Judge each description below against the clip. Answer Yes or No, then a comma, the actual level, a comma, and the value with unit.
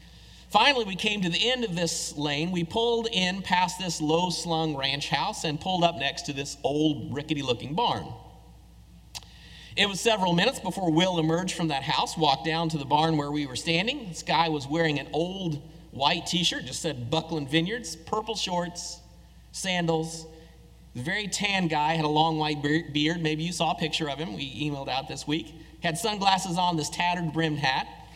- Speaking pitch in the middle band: Yes, medium, 165 Hz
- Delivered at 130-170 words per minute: No, average, 195 wpm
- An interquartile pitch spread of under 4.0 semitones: Yes, average, 2.9 semitones